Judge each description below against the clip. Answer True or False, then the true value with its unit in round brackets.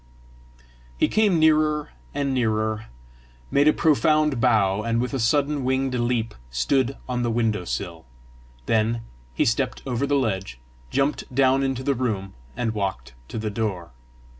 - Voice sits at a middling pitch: False (125 Hz)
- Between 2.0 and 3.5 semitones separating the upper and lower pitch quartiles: False (4.1 semitones)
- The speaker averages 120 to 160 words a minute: True (150 wpm)